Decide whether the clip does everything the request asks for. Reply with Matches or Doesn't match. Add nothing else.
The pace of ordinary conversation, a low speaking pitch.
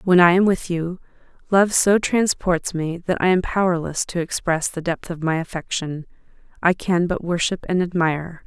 Doesn't match